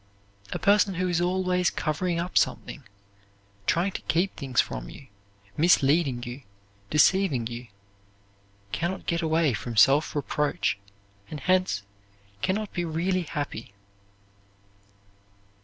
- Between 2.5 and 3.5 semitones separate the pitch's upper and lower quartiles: No, average, 4.9 semitones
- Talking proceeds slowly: Yes, slow, 125 wpm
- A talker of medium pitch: Yes, medium, 165 Hz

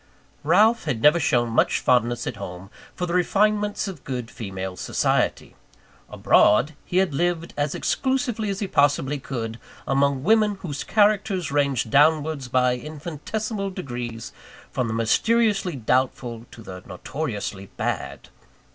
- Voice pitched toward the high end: No, medium, 145 Hz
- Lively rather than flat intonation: Yes, wide, 7.9 semitones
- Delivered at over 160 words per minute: No, slow, 135 wpm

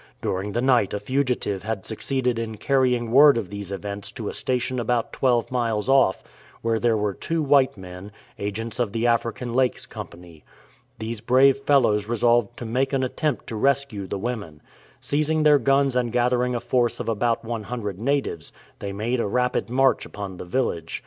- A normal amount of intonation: Yes, average, 3.9 semitones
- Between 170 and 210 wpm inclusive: Yes, average, 180 wpm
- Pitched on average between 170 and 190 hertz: No, low, 120 Hz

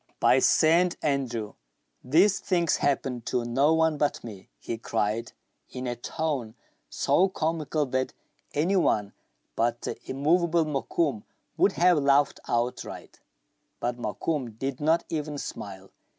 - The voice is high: No, medium, 140 Hz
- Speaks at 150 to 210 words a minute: No, slow, 135 wpm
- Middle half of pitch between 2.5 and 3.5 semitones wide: No, average, 5.1 semitones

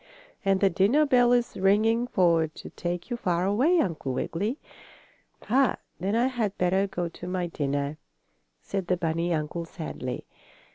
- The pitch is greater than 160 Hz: Yes, medium, 185 Hz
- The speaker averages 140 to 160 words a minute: Yes, average, 155 wpm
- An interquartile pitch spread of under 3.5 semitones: No, average, 5.1 semitones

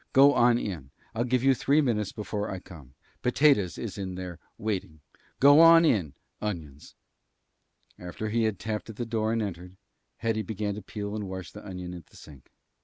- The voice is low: Yes, low, 105 Hz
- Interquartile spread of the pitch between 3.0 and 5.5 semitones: Yes, average, 4.2 semitones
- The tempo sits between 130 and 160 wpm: No, average, 185 wpm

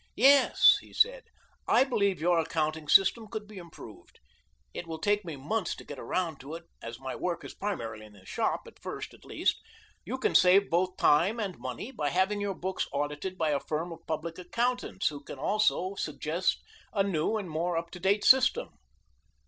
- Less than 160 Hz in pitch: No, medium, 180 Hz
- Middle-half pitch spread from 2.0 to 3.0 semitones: No, average, 4.9 semitones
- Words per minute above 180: Yes, average, 195 wpm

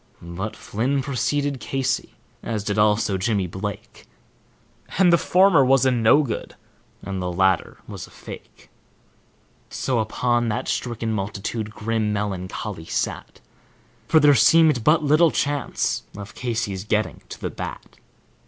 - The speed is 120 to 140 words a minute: Yes, slow, 135 wpm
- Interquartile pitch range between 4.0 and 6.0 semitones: Yes, average, 5.0 semitones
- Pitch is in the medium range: No, low, 115 Hz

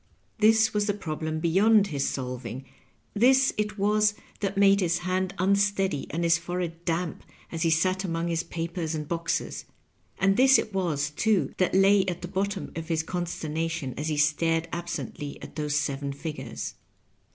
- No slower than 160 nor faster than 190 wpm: Yes, average, 165 wpm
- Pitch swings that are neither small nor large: Yes, average, 3.7 semitones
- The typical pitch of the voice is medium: Yes, medium, 170 Hz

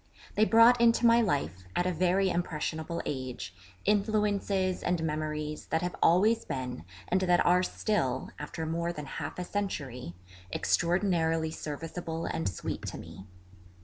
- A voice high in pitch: No, medium, 170 Hz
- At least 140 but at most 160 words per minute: Yes, average, 145 wpm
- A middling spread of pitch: Yes, average, 4.2 semitones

